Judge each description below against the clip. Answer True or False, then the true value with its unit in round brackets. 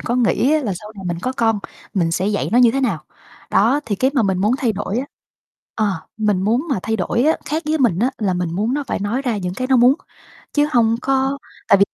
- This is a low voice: False (225 Hz)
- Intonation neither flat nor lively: True (4.7 semitones)